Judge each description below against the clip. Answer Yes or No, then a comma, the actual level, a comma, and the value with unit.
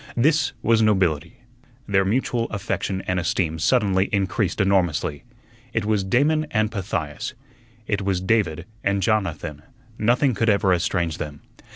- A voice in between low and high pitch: No, low, 100 Hz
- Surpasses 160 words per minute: No, slow, 135 wpm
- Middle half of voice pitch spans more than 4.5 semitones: No, average, 3.9 semitones